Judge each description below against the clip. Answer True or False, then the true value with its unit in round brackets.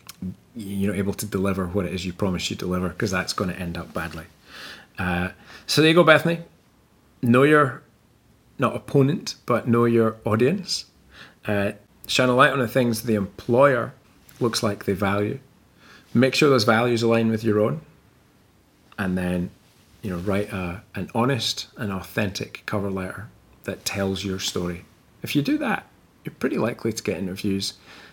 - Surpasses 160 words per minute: True (170 wpm)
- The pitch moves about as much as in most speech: True (4.0 semitones)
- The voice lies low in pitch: True (105 Hz)